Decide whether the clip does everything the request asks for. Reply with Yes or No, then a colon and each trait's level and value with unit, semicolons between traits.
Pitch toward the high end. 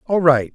No: medium, 155 Hz